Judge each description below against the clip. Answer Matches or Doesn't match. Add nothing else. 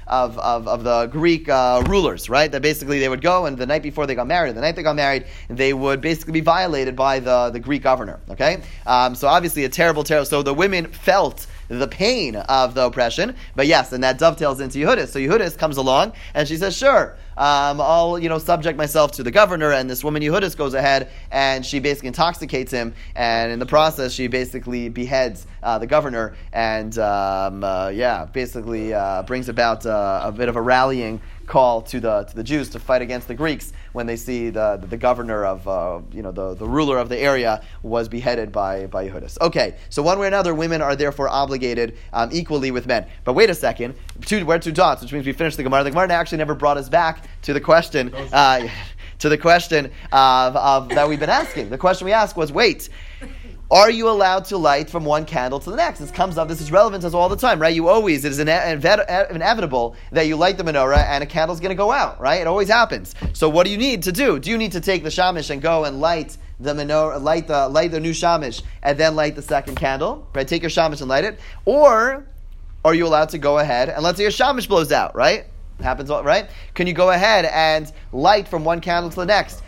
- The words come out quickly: Matches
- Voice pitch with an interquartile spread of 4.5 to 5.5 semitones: Matches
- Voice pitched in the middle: Matches